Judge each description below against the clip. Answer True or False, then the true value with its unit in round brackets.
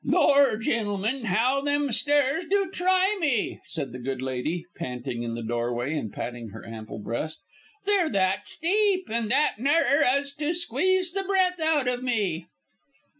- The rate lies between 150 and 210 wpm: True (160 wpm)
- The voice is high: True (250 Hz)